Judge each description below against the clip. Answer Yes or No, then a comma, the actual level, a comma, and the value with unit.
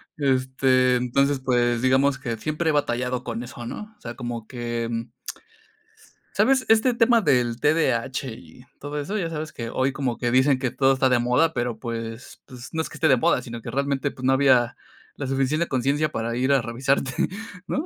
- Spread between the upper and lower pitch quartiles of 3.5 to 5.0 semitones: No, average, 2.9 semitones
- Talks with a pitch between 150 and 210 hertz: No, low, 130 Hz